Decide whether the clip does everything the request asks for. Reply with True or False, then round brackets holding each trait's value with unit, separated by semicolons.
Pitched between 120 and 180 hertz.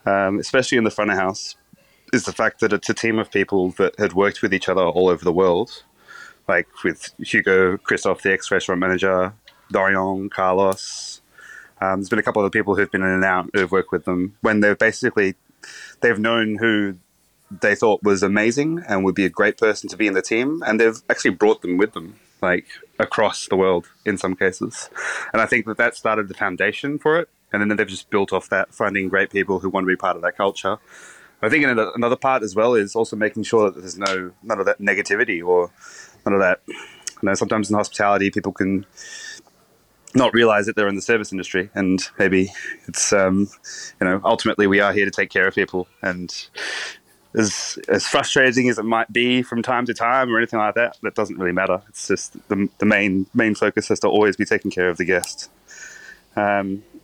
False (100 Hz)